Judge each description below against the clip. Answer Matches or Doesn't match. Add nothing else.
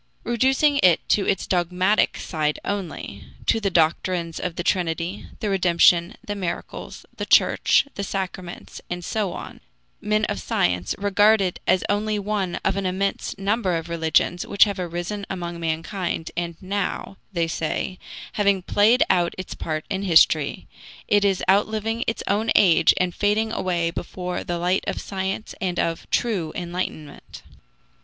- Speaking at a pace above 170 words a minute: Doesn't match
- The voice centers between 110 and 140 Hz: Doesn't match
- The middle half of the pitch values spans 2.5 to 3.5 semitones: Matches